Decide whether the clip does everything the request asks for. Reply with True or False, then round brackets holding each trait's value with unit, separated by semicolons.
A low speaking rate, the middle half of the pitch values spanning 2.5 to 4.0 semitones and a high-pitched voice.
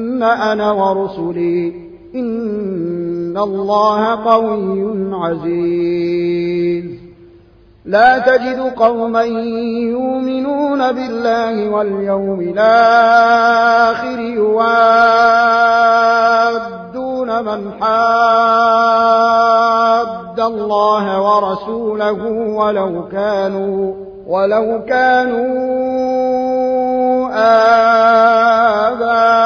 True (45 wpm; 2.8 semitones; 225 Hz)